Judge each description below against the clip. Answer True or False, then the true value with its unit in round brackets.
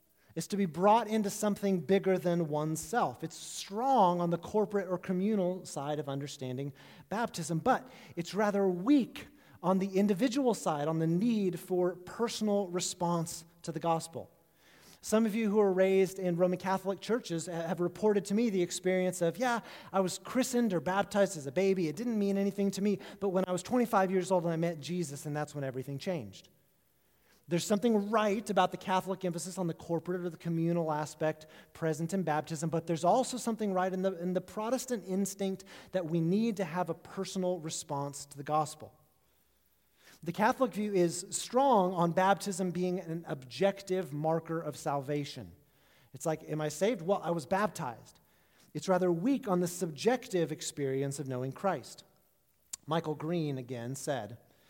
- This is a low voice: False (180 Hz)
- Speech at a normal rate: True (175 wpm)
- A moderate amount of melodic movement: True (3.5 semitones)